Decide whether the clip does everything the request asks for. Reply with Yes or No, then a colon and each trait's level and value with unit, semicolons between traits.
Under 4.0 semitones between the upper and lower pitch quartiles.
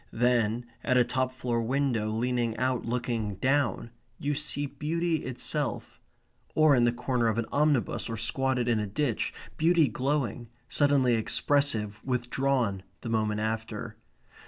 Yes: average, 3.6 semitones